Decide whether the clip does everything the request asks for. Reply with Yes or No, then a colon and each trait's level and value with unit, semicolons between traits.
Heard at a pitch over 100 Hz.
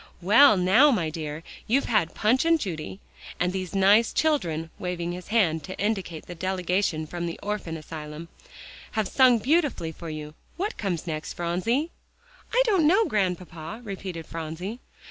Yes: medium, 185 Hz